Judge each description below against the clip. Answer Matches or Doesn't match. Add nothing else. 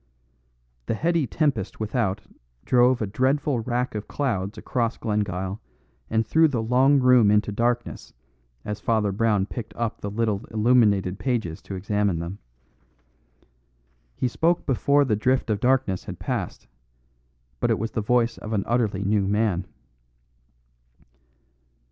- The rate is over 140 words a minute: Doesn't match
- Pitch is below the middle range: Matches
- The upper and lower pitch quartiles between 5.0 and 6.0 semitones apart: Doesn't match